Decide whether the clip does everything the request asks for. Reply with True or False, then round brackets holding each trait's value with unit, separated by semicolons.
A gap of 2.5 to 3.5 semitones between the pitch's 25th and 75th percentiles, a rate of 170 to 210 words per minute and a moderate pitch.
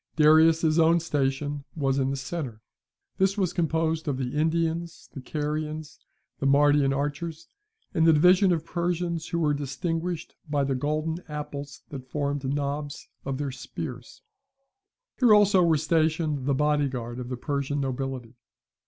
False (2.9 semitones; 150 wpm; 150 Hz)